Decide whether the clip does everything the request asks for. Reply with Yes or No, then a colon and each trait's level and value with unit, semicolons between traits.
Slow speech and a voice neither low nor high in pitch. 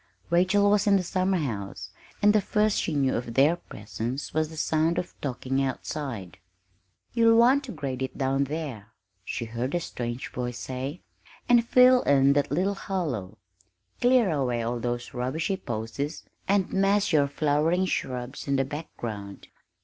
No: average, 155 wpm; medium, 145 Hz